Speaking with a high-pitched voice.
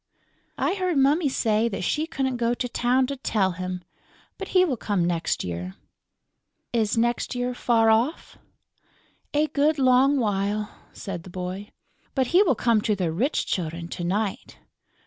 Yes: high, 230 Hz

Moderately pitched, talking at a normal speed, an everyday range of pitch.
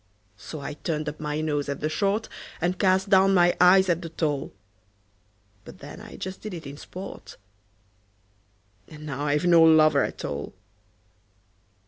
Yes: medium, 160 Hz; average, 160 wpm; average, 3.8 semitones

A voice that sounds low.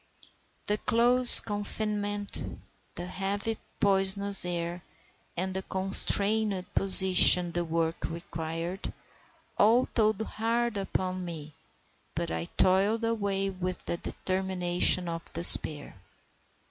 No: high, 190 Hz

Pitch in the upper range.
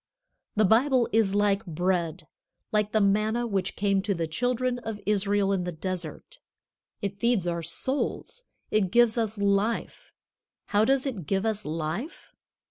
Yes: high, 205 Hz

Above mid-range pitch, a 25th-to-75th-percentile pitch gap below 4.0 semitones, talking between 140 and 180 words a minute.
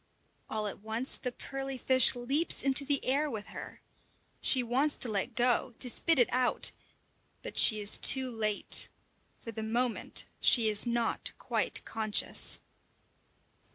Yes: high, 245 Hz; average, 3.1 semitones; average, 150 wpm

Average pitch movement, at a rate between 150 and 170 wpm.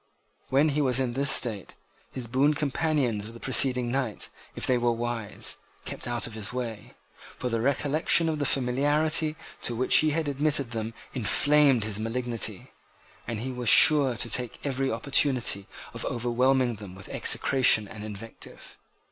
Yes: average, 3.4 semitones; average, 165 wpm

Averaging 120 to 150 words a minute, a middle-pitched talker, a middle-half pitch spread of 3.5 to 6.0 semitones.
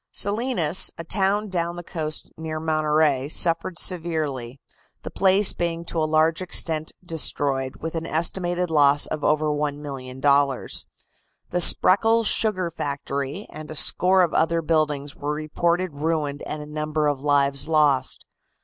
No: average, 140 wpm; medium, 155 Hz; average, 3.0 semitones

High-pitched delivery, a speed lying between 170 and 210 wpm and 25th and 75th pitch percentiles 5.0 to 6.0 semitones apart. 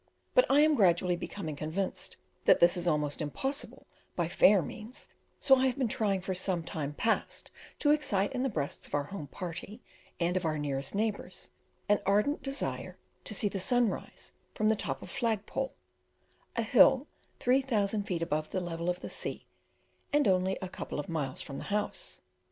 Yes: high, 195 Hz; average, 185 wpm; wide, 5.4 semitones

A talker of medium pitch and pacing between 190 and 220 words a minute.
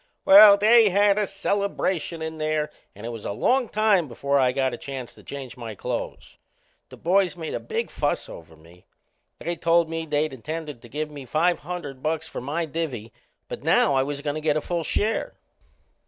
Yes: medium, 155 Hz; average, 200 wpm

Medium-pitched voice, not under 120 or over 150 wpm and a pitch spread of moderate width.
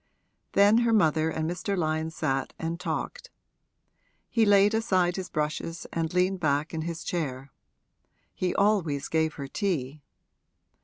Yes: medium, 165 Hz; average, 140 wpm; average, 3.9 semitones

